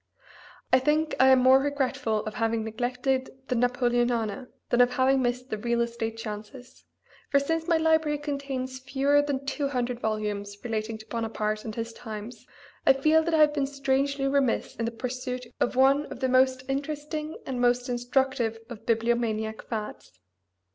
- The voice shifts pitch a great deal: No, average, 3.3 semitones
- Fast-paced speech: No, average, 170 wpm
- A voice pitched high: Yes, very high, 250 Hz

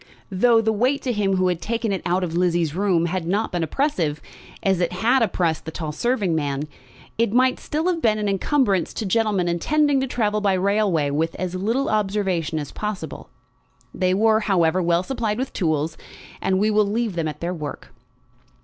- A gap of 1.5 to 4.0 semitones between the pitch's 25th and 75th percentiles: No, average, 4.6 semitones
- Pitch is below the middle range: No, high, 195 Hz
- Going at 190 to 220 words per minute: Yes, average, 195 wpm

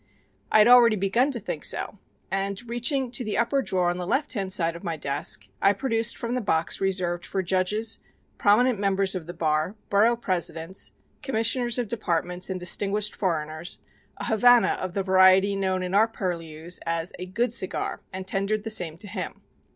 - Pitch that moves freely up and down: No, average, 4.1 semitones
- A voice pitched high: Yes, high, 195 Hz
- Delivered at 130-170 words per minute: No, average, 185 wpm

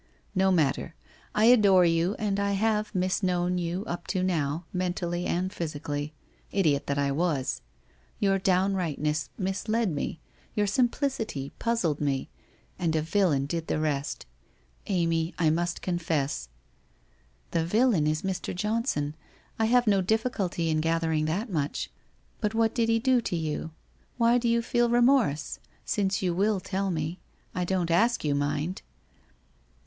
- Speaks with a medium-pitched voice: Yes, medium, 180 Hz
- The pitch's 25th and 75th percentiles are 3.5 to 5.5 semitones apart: Yes, average, 5.0 semitones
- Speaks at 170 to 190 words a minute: No, average, 155 wpm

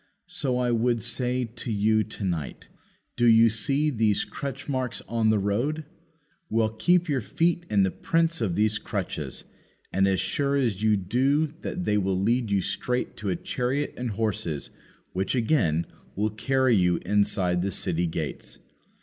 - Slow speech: No, average, 165 wpm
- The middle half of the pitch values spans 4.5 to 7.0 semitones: Yes, average, 4.8 semitones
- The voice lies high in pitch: No, low, 110 Hz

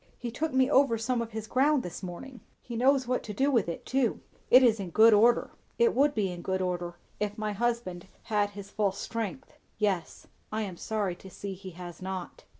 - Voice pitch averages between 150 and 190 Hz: No, high, 215 Hz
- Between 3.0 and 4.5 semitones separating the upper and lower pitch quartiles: No, average, 4.9 semitones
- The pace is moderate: No, fast, 215 wpm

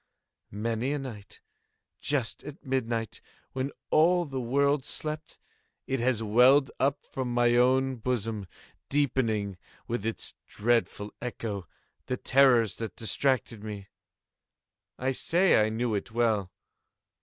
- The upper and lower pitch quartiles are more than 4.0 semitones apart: No, average, 3.4 semitones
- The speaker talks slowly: Yes, slow, 120 wpm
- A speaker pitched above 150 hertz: No, low, 120 Hz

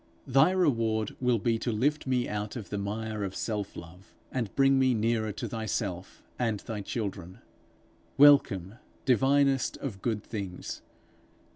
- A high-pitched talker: No, low, 110 Hz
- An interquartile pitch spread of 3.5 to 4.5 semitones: Yes, average, 4.1 semitones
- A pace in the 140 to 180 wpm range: Yes, average, 145 wpm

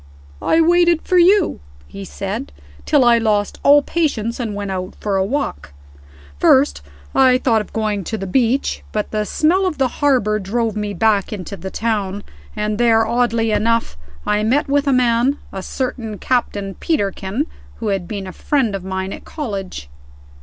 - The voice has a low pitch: No, high, 220 Hz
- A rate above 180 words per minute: No, average, 175 wpm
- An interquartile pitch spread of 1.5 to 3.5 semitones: No, average, 4.6 semitones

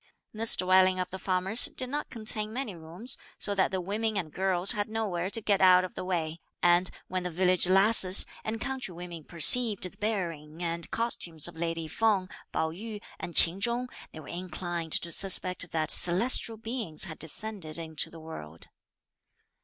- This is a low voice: No, medium, 185 Hz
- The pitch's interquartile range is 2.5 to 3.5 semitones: No, average, 4.2 semitones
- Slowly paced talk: No, average, 175 wpm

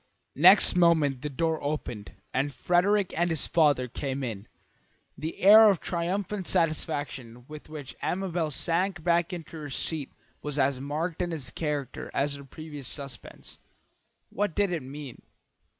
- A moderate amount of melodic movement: Yes, average, 3.8 semitones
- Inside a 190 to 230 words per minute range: No, average, 150 wpm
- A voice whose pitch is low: No, medium, 155 Hz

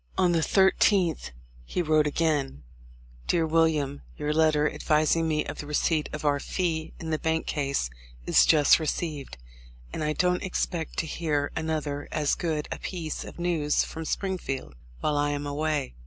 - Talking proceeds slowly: No, average, 170 wpm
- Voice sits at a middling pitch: Yes, medium, 155 Hz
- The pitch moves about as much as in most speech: No, narrow, 1.9 semitones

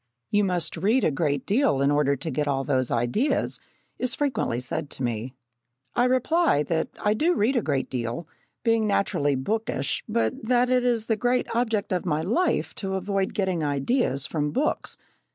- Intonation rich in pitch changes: Yes, wide, 9.0 semitones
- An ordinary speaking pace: Yes, average, 180 wpm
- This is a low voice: No, high, 190 Hz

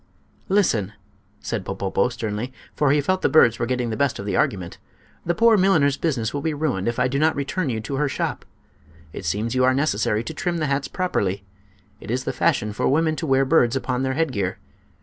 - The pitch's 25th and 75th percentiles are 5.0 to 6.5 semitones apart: Yes, wide, 5.6 semitones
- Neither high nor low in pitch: No, low, 130 Hz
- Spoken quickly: Yes, fast, 215 wpm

